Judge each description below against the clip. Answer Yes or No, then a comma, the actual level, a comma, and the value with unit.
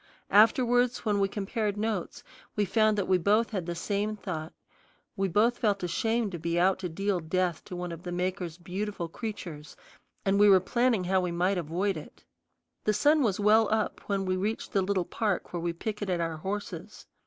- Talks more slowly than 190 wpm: No, average, 195 wpm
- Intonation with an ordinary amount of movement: Yes, average, 3.1 semitones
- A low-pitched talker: No, high, 195 Hz